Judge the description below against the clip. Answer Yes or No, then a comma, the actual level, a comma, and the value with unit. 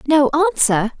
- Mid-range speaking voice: No, very high, 260 Hz